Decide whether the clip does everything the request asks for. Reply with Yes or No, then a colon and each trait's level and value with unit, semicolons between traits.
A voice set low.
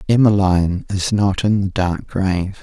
Yes: very low, 95 Hz